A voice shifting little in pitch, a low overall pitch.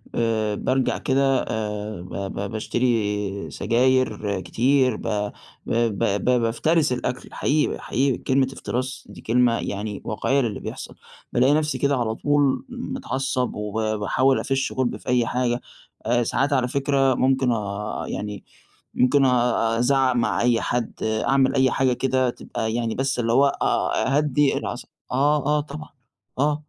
No: average, 3.4 semitones; low, 125 Hz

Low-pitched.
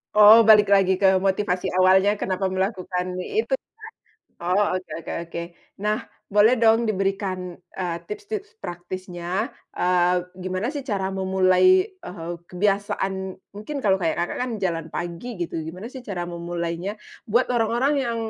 No: high, 190 Hz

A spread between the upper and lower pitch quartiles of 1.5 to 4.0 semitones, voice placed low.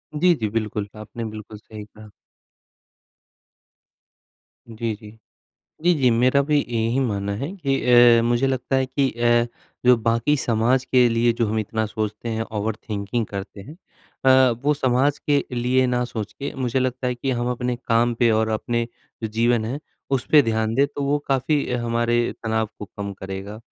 Yes: average, 2.9 semitones; low, 120 Hz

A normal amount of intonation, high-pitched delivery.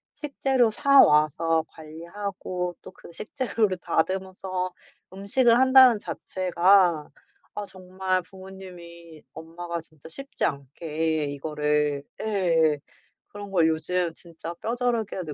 No: average, 3.8 semitones; medium, 180 Hz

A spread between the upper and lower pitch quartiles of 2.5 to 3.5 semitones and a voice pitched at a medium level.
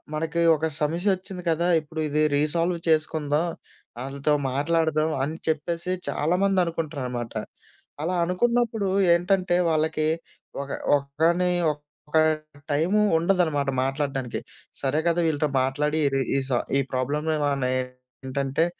Yes: average, 3.1 semitones; medium, 155 Hz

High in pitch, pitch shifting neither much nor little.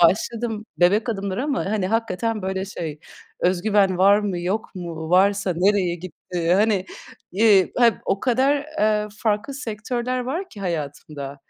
Yes: high, 200 Hz; average, 3.8 semitones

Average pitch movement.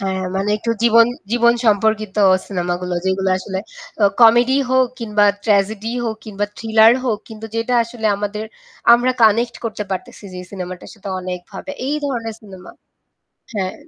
Yes: average, 3.1 semitones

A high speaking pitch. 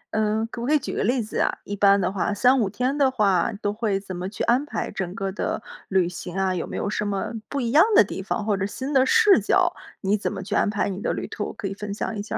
Yes: high, 205 Hz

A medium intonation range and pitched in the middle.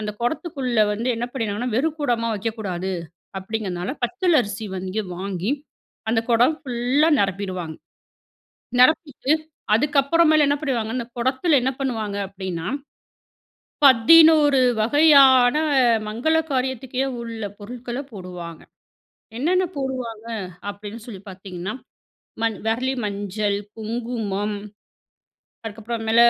No: average, 4.6 semitones; high, 230 Hz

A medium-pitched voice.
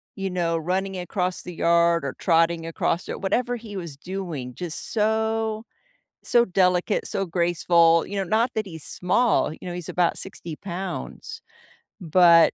Yes: medium, 180 Hz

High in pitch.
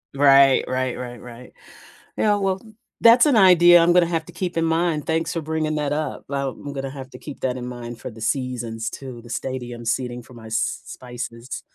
No: low, 135 Hz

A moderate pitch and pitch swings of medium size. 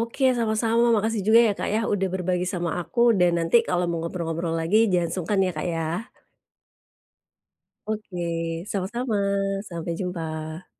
Yes: medium, 180 Hz; average, 4.5 semitones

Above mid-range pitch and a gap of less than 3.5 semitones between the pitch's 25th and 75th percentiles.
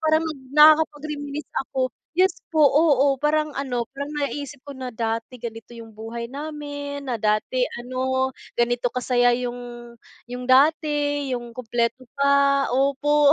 Yes: very high, 275 Hz; average, 3.1 semitones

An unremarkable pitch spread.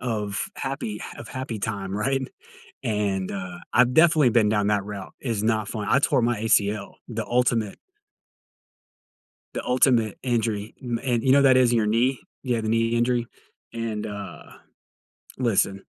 Yes: average, 3.0 semitones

